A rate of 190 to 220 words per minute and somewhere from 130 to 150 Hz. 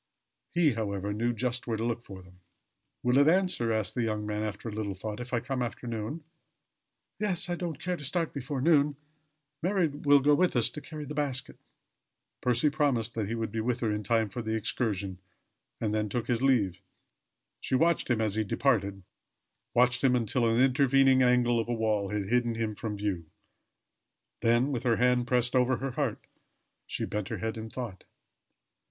No: average, 195 wpm; low, 120 Hz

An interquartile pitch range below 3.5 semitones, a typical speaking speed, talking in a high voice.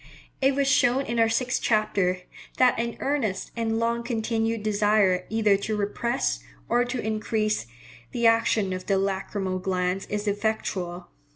Yes: average, 3.1 semitones; average, 150 wpm; high, 215 Hz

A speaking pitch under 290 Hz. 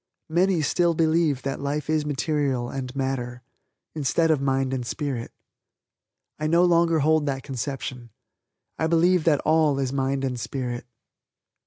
Yes: medium, 140 Hz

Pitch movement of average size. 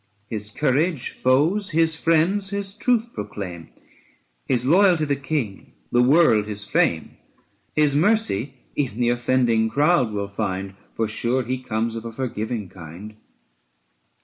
No: wide, 6.7 semitones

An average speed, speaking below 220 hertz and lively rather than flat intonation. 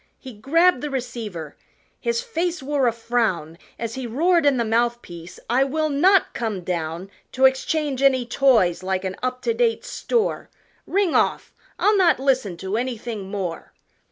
No: average, 165 wpm; very high, 250 Hz; wide, 6.5 semitones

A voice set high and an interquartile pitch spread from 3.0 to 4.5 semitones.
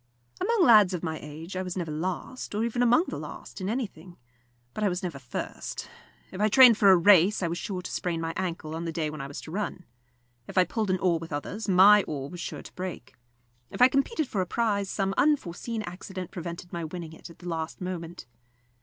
No: medium, 180 Hz; average, 3.9 semitones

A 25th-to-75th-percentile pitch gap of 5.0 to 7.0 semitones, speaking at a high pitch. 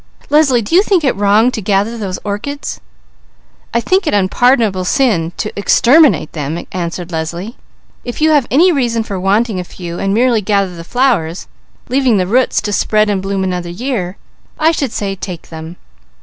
Yes: wide, 5.5 semitones; high, 205 Hz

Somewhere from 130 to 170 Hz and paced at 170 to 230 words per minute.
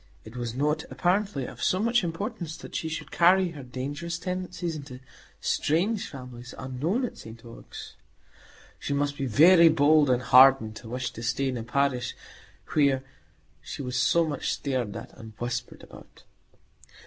No: medium, 140 Hz; average, 160 wpm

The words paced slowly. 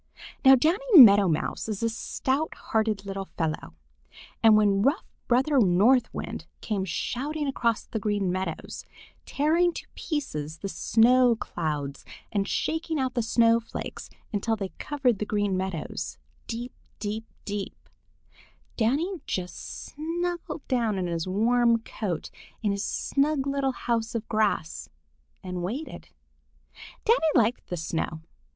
Yes: slow, 130 wpm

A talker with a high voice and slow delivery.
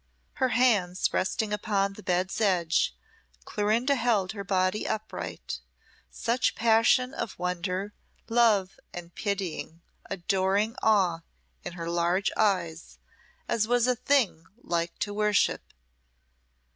Yes: high, 200 Hz; slow, 115 wpm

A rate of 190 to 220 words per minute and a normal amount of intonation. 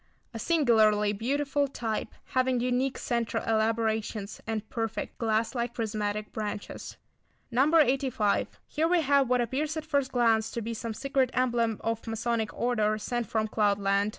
No: average, 150 wpm; average, 3.2 semitones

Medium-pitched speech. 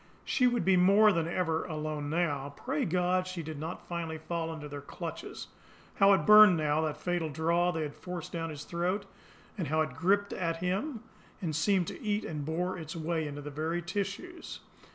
Yes: medium, 170 Hz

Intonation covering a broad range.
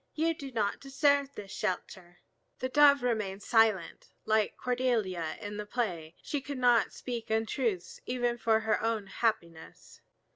No: average, 3.9 semitones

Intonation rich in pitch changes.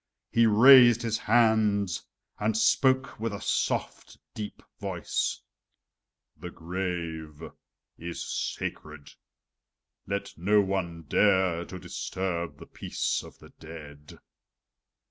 No: average, 4.7 semitones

